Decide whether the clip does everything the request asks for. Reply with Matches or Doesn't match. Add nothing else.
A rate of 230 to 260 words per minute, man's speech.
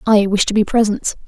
Doesn't match